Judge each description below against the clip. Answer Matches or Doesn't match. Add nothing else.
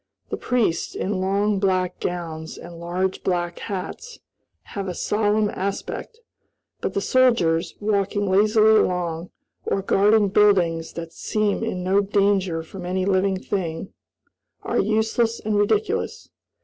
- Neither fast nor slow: Doesn't match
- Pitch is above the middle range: Matches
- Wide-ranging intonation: Doesn't match